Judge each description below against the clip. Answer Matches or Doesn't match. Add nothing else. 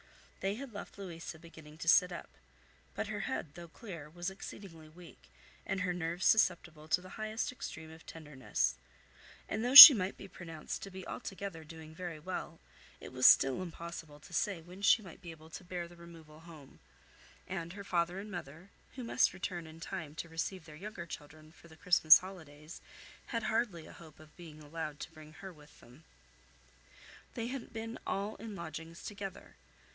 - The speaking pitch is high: Doesn't match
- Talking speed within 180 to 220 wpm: Matches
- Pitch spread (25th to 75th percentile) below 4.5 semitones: Matches